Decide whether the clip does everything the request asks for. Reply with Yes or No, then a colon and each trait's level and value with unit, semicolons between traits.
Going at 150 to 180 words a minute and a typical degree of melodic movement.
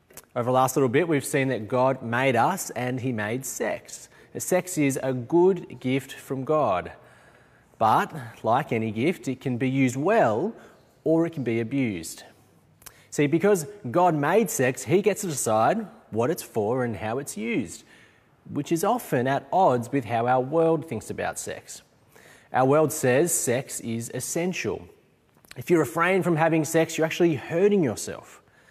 Yes: average, 170 wpm; average, 4.7 semitones